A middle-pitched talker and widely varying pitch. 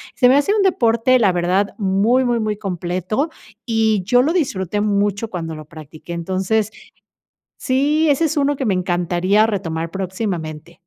No: high, 205 Hz; wide, 5.7 semitones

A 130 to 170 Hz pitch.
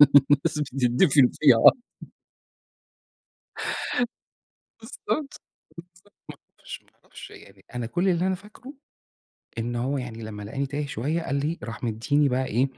Yes: medium, 140 Hz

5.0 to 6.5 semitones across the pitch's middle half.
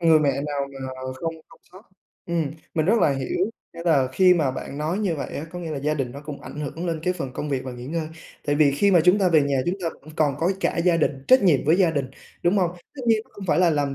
No: average, 4.0 semitones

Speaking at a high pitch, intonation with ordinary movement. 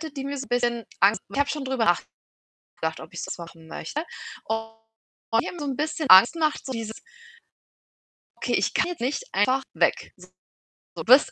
Yes: very high, 255 Hz; average, 4.4 semitones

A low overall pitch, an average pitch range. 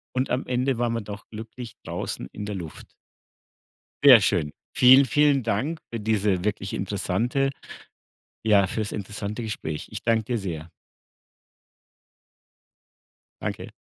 Yes: low, 110 Hz; average, 3.7 semitones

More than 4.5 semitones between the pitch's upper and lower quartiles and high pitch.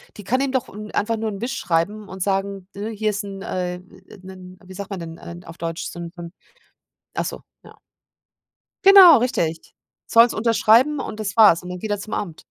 No: average, 3.5 semitones; high, 200 Hz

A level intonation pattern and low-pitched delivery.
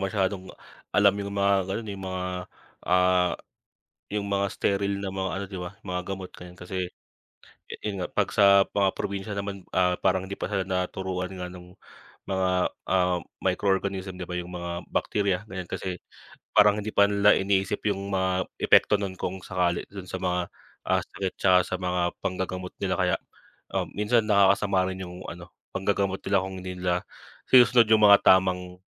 Yes: narrow, 1.5 semitones; very low, 95 Hz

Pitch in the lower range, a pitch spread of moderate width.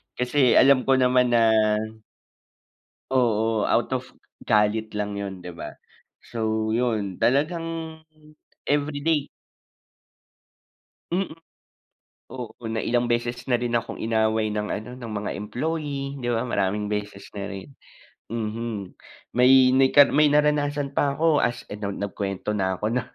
Yes: low, 120 Hz; average, 4.7 semitones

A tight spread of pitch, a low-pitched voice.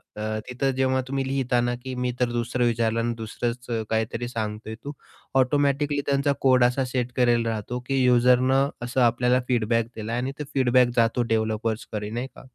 Yes: narrow, 2.2 semitones; low, 125 Hz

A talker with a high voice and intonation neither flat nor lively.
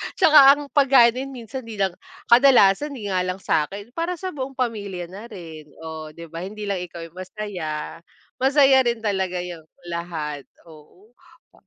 No: high, 200 Hz; wide, 6.3 semitones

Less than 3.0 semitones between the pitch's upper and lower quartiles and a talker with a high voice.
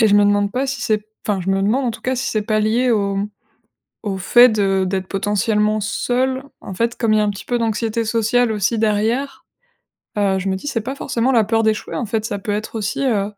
Yes: narrow, 2.6 semitones; high, 215 Hz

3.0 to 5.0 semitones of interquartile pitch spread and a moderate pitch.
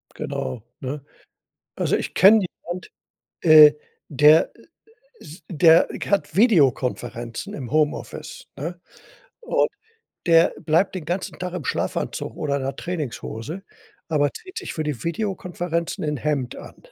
Yes: average, 3.7 semitones; medium, 155 Hz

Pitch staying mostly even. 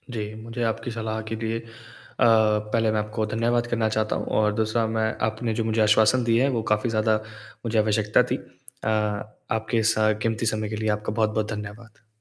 Yes: narrow, 1.0 semitones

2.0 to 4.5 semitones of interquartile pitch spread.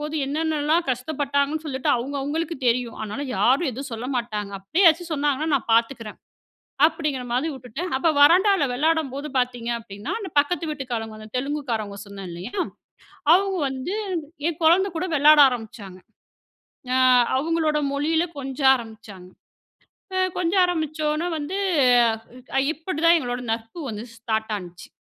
No: wide, 5.4 semitones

